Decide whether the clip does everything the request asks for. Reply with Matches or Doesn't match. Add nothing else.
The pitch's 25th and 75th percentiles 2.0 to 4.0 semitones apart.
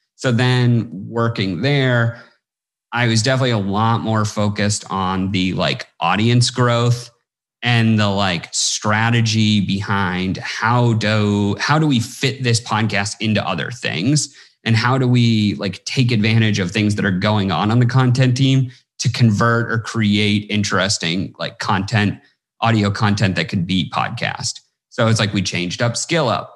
Matches